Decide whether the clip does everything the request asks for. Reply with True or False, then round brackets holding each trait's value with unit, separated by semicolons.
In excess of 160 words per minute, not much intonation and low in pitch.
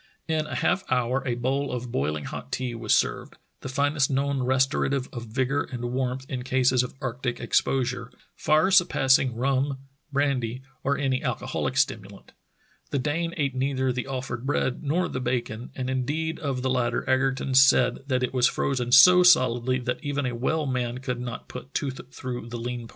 True (185 wpm; 1.9 semitones; 130 Hz)